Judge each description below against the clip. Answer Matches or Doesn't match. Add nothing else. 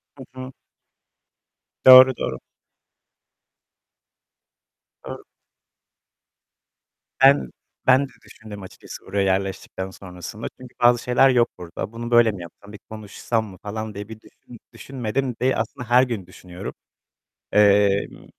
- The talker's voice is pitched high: Doesn't match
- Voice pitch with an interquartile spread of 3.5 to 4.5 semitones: Matches